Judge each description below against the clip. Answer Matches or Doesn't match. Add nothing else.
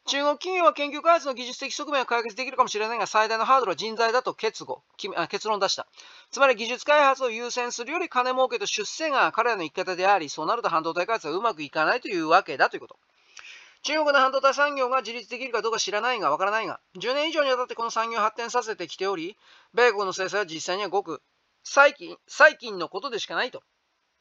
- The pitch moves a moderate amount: Matches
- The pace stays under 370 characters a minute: Doesn't match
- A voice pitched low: Doesn't match